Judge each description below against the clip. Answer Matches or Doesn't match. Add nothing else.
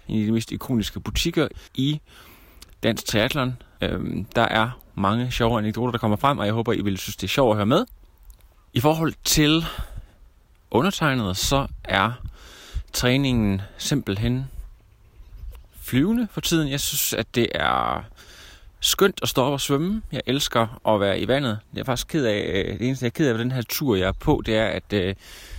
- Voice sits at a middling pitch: Doesn't match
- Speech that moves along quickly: Doesn't match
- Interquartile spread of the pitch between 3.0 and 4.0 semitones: Doesn't match